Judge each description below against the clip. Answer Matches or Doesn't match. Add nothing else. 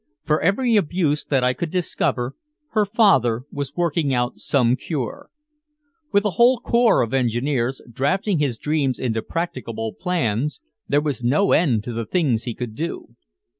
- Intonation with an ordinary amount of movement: Doesn't match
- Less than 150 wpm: Doesn't match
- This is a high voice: Doesn't match